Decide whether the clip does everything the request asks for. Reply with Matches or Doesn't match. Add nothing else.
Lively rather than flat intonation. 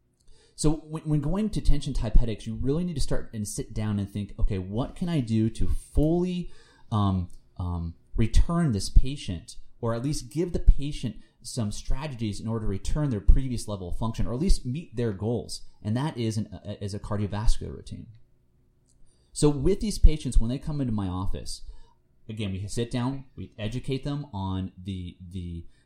Matches